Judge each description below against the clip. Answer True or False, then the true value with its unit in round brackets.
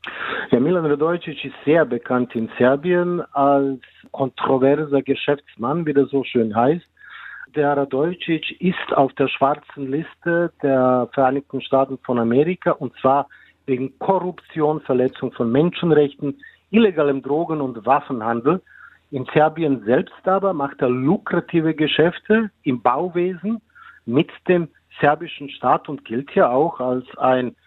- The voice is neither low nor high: True (145 Hz)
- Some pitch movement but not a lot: True (3.9 semitones)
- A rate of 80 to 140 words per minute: True (130 wpm)